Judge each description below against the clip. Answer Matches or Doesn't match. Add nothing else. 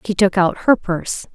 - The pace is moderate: Doesn't match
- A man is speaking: Doesn't match